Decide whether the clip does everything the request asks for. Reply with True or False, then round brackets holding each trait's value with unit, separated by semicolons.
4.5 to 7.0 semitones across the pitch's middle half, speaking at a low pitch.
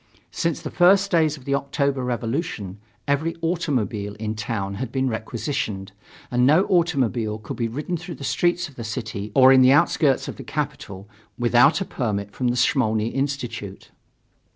True (5.1 semitones; 130 Hz)